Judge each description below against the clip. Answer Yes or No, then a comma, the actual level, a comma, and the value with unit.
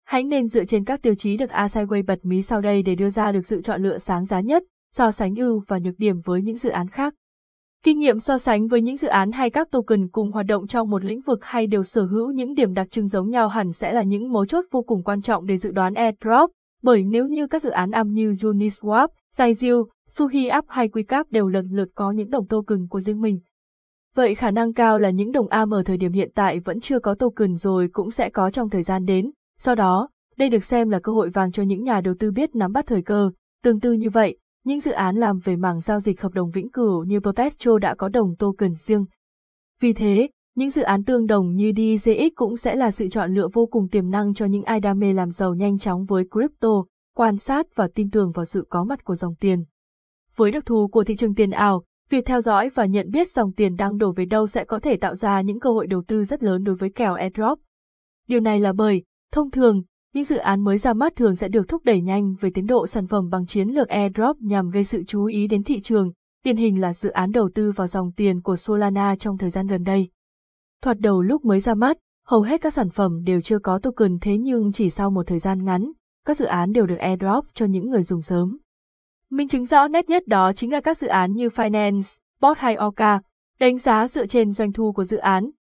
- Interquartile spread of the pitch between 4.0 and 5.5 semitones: No, average, 3.5 semitones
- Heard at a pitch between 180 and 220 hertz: Yes, high, 215 Hz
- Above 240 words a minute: Yes, fast, 250 wpm